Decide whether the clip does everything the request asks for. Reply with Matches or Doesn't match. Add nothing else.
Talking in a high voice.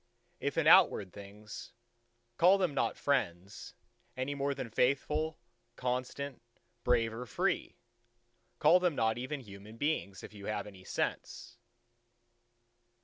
Doesn't match